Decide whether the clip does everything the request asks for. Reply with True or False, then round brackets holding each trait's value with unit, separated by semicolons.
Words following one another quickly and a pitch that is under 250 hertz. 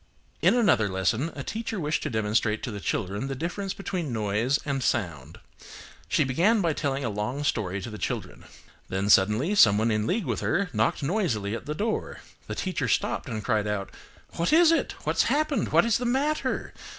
False (185 wpm; 135 Hz)